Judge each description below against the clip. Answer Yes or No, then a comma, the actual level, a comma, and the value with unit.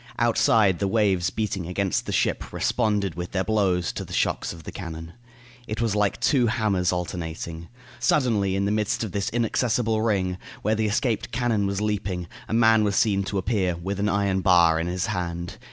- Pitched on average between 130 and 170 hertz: No, low, 100 Hz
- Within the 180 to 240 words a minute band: Yes, average, 190 wpm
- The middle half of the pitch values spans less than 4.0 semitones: Yes, average, 3.3 semitones